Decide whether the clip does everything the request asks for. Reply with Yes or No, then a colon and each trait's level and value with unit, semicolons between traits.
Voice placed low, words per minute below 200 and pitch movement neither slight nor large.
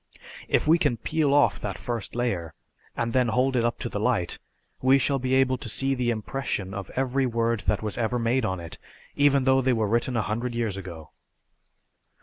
No: low, 120 Hz; fast, 205 wpm; average, 3.4 semitones